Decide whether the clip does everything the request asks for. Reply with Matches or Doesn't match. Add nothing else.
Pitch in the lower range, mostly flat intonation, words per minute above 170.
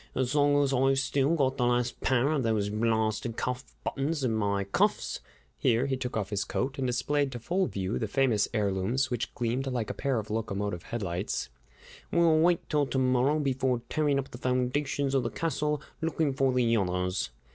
Doesn't match